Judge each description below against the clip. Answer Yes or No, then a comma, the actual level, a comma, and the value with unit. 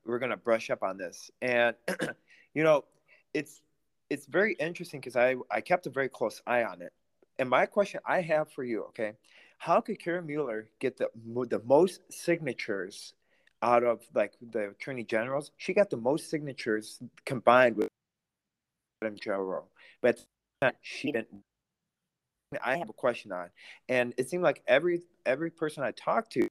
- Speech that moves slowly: No, average, 165 wpm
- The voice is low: No, medium, 145 Hz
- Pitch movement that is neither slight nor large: No, wide, 6.7 semitones